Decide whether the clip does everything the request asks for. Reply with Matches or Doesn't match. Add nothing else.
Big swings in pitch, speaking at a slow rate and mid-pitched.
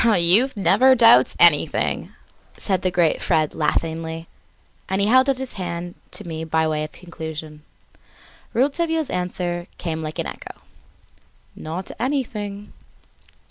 Matches